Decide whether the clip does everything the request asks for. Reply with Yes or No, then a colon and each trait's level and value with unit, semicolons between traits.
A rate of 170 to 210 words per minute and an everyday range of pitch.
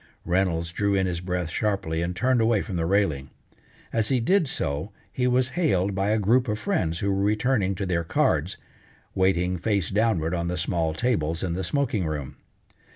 Yes: average, 190 wpm; average, 4.5 semitones